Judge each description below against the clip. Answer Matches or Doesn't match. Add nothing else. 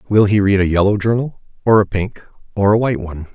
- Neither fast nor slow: Doesn't match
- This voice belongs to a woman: Doesn't match